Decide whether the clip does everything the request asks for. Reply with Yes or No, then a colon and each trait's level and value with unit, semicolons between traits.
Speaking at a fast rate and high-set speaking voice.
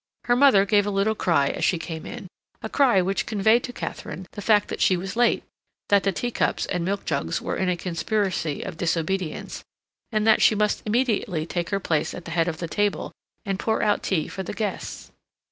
Yes: fast, 215 wpm; high, 195 Hz